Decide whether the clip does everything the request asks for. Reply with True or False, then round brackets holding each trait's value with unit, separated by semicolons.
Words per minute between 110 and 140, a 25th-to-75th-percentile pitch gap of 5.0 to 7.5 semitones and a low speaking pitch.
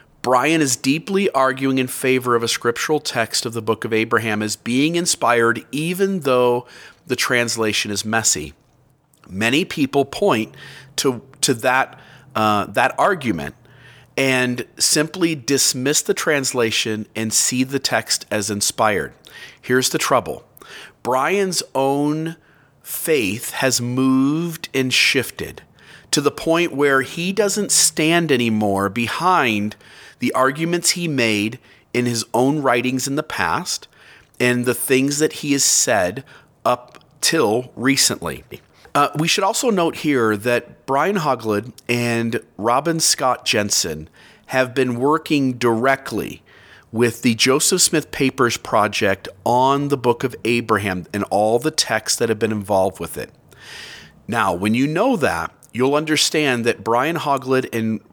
False (135 wpm; 4.2 semitones; 130 Hz)